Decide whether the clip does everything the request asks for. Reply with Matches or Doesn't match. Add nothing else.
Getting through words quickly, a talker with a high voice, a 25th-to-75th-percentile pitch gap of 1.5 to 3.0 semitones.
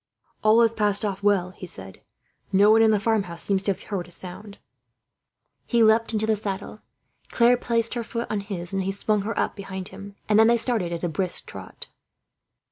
Matches